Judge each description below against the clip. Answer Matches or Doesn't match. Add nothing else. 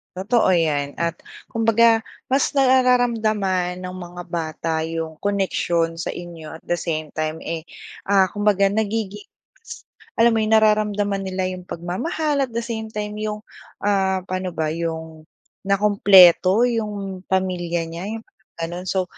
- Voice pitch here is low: Doesn't match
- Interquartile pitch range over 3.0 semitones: Matches